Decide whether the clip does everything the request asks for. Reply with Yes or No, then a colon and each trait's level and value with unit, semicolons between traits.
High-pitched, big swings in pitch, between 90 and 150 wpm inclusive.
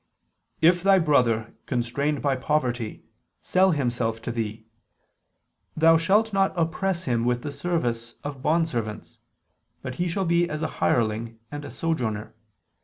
No: medium, 145 Hz; wide, 6.1 semitones; average, 140 wpm